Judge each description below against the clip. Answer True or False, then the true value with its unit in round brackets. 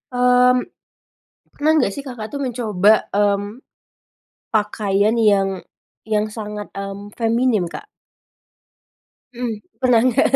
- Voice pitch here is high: True (215 Hz)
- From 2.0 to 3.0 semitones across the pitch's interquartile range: False (3.5 semitones)